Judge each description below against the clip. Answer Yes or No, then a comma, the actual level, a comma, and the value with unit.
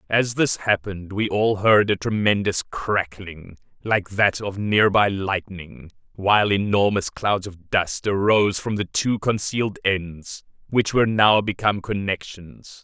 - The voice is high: No, low, 100 Hz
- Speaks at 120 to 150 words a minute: Yes, average, 140 wpm